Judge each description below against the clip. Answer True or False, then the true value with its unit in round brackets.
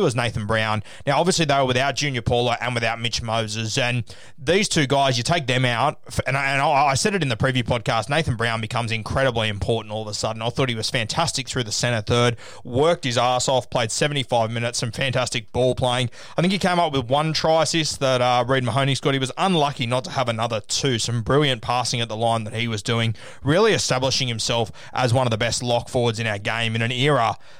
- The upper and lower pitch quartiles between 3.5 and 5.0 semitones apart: False (2.9 semitones)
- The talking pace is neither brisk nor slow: False (240 wpm)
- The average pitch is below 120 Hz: False (125 Hz)